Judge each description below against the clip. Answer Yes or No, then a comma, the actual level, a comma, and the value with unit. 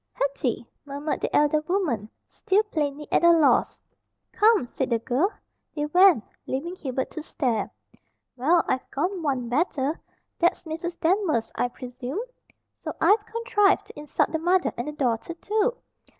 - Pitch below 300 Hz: No, very high, 305 Hz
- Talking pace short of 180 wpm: Yes, average, 150 wpm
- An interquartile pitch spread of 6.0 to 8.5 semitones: No, wide, 5.6 semitones